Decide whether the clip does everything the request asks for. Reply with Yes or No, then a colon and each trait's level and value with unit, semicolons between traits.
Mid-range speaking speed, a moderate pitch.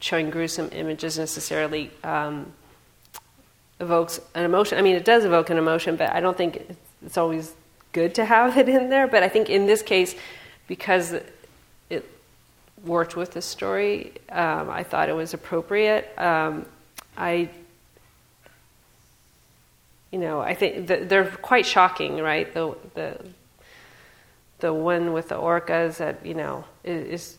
Yes: average, 145 wpm; medium, 170 Hz